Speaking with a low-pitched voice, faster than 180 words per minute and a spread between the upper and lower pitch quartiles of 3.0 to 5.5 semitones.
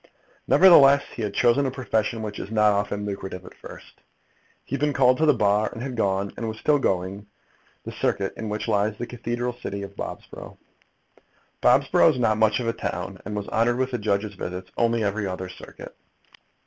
Yes: low, 110 Hz; average, 200 wpm; average, 3.4 semitones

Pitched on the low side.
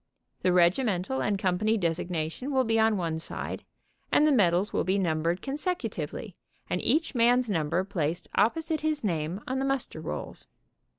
No: high, 200 Hz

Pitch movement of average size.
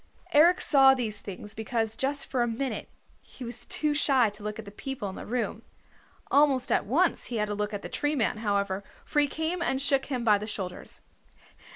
Yes: average, 4.8 semitones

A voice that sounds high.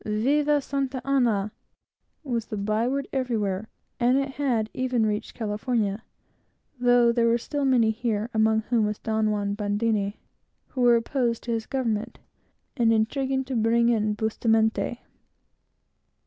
Yes: high, 230 Hz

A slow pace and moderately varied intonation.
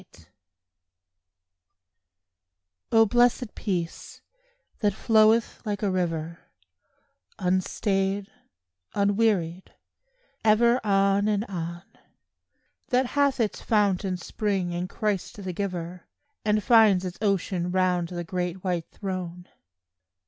Yes: slow, 100 wpm; average, 3.0 semitones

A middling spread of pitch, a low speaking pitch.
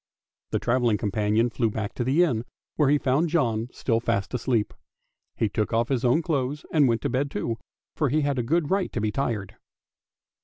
Yes: average, 4.3 semitones; low, 125 Hz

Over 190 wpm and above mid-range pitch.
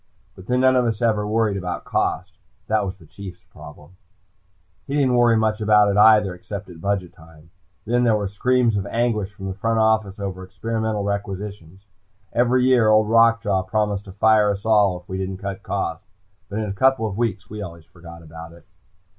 No: average, 200 wpm; low, 105 Hz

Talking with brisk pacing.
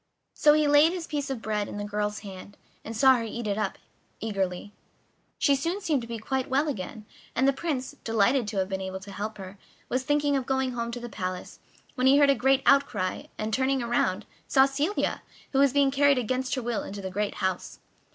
Yes: fast, 220 wpm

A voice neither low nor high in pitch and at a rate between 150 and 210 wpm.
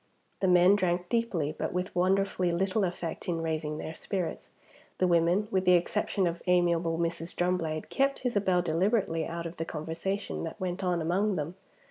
Yes: medium, 175 Hz; average, 170 wpm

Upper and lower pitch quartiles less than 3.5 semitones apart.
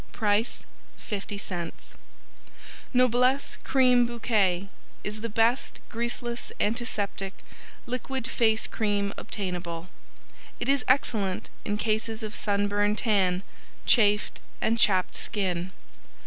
Yes: average, 3.1 semitones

